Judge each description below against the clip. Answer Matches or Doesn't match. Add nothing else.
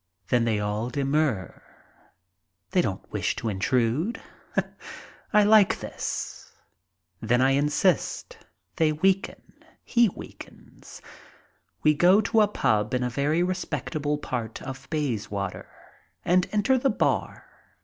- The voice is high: Doesn't match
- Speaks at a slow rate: Matches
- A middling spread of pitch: Doesn't match